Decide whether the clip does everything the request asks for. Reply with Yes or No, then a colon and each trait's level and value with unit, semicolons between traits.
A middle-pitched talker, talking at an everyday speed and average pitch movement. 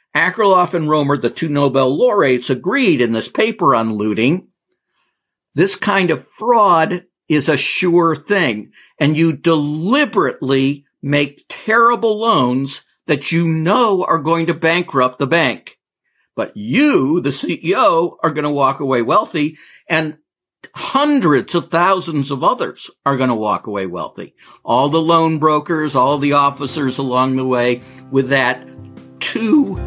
Yes: medium, 150 Hz; average, 145 wpm; average, 4.1 semitones